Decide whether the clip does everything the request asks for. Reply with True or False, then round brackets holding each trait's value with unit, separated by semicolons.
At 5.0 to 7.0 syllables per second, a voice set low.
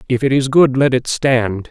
False (4.6 syllables/s; 130 Hz)